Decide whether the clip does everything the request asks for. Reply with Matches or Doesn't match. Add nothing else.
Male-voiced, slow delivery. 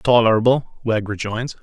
Matches